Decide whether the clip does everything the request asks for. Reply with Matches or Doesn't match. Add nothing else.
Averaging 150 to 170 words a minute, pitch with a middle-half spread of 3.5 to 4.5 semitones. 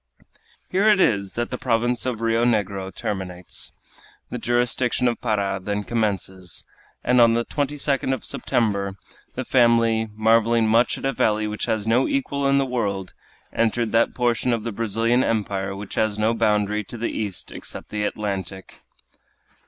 Doesn't match